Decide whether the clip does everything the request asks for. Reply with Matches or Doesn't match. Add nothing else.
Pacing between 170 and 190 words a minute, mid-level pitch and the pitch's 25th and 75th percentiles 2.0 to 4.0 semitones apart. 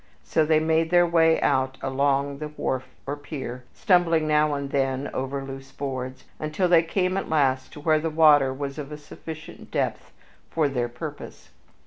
Matches